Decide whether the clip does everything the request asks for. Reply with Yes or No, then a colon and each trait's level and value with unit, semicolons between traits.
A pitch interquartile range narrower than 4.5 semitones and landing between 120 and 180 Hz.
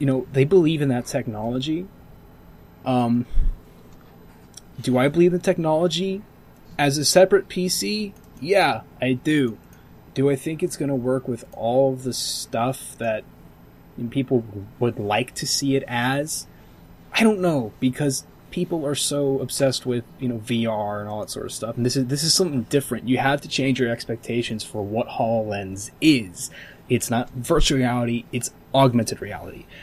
Yes: average, 3.8 semitones; low, 130 Hz